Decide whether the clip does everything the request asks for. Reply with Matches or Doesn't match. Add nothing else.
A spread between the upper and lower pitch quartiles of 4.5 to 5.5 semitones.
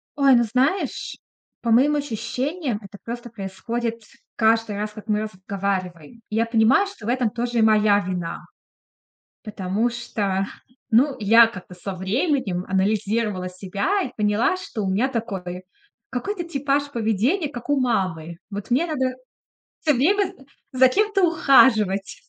Matches